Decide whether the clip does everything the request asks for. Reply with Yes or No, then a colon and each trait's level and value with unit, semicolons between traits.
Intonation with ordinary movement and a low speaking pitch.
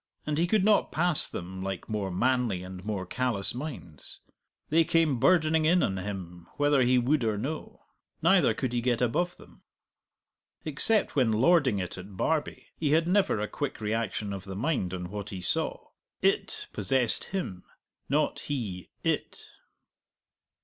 No: wide, 8.0 semitones; low, 120 Hz